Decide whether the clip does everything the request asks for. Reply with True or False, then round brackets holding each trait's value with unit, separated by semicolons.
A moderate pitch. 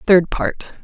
True (180 Hz)